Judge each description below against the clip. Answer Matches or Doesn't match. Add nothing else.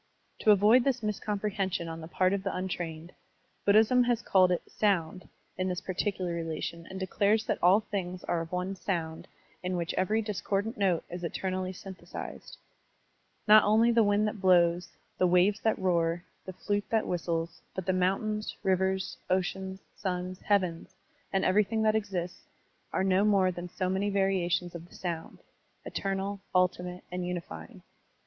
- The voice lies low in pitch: Doesn't match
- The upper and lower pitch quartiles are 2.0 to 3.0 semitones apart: Matches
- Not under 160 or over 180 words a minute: Matches